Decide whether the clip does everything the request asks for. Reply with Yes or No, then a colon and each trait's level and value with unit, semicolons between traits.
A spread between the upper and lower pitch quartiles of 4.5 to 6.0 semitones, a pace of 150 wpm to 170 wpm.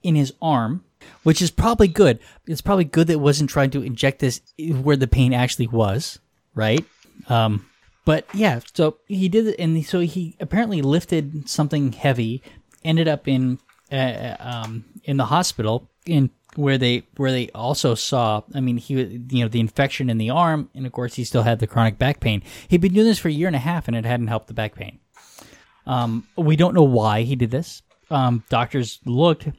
No: average, 5.1 semitones; fast, 205 wpm